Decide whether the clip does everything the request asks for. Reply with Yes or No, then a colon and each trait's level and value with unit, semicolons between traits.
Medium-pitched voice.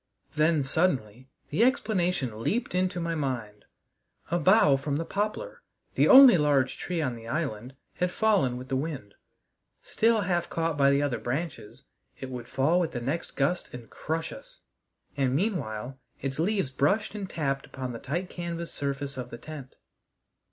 Yes: medium, 145 Hz